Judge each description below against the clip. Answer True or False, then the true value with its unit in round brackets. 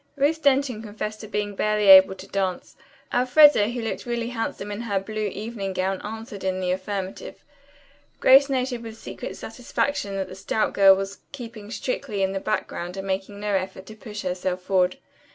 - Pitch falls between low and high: False (210 Hz)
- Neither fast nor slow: True (180 wpm)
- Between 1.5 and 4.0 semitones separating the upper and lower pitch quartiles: True (3.5 semitones)